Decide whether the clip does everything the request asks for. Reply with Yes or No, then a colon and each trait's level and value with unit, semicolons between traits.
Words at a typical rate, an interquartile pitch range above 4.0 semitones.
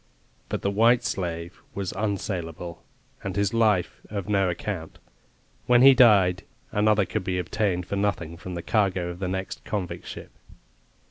No: average, 155 wpm; average, 2.8 semitones